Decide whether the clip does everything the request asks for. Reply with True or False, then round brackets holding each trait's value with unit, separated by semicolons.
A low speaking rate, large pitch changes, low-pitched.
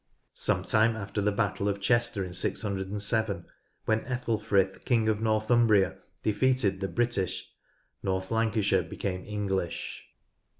False (120 wpm; 2.6 semitones; 105 Hz)